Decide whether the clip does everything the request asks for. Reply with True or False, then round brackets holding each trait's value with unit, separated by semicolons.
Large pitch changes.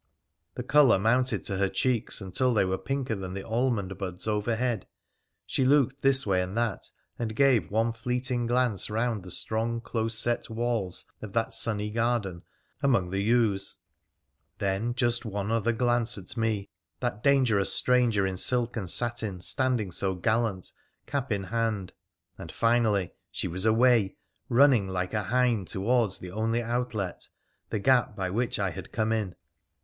False (3.7 semitones)